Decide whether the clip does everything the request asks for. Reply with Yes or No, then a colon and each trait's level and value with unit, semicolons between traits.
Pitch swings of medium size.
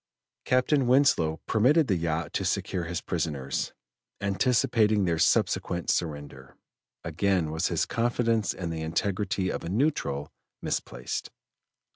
No: wide, 6.2 semitones